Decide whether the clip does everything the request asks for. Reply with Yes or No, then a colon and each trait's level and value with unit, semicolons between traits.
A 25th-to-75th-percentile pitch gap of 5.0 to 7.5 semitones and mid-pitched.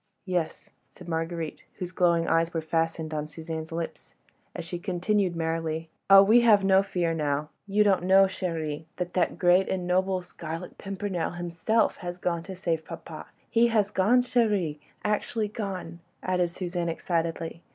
No: average, 2.8 semitones; medium, 175 Hz